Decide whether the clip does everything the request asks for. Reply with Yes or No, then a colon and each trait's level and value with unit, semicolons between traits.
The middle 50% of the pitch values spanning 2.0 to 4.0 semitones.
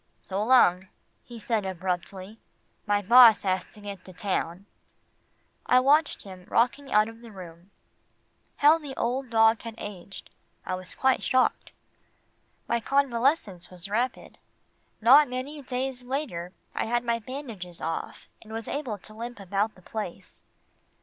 No: average, 5.0 semitones